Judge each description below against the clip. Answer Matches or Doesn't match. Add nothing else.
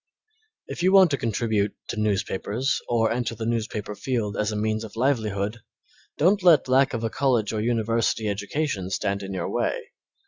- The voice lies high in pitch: Doesn't match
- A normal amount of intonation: Matches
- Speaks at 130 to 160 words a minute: Doesn't match